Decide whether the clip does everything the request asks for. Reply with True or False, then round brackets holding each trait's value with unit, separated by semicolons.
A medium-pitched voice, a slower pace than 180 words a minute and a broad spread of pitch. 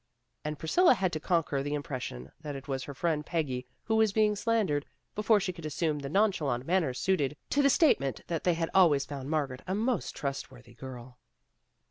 False (155 Hz; 200 wpm; 5.7 semitones)